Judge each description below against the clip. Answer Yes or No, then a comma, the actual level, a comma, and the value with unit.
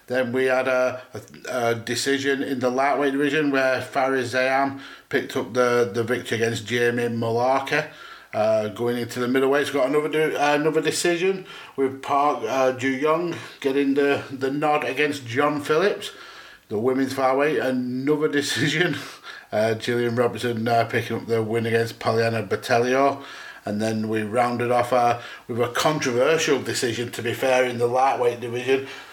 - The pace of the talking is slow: No, average, 165 wpm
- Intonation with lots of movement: No, average, 2.7 semitones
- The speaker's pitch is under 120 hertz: No, low, 130 Hz